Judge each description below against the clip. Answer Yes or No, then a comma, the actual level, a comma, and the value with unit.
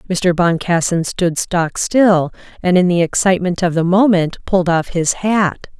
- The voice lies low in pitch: No, medium, 180 Hz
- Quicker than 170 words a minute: No, average, 165 wpm